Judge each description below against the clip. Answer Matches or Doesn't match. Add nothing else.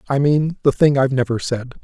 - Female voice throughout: Doesn't match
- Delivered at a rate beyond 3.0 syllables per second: Matches